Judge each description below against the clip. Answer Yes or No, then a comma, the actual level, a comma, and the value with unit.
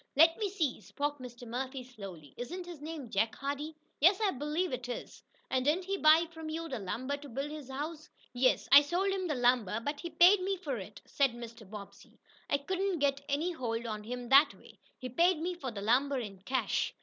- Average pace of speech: No, fast, 210 wpm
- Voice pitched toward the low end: No, very high, 280 Hz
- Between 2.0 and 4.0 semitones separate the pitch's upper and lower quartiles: No, average, 5.0 semitones